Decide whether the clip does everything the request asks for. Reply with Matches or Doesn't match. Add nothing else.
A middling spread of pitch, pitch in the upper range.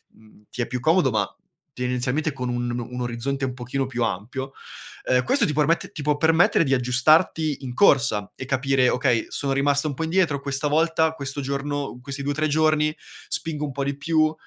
Doesn't match